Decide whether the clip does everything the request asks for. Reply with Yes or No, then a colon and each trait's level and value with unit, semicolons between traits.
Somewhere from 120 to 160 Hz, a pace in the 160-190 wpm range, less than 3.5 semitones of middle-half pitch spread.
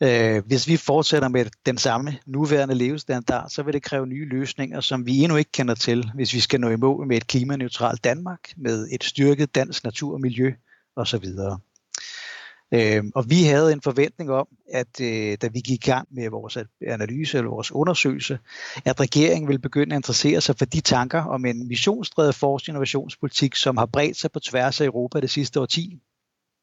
Yes: low, 135 Hz; average, 185 wpm; average, 3.0 semitones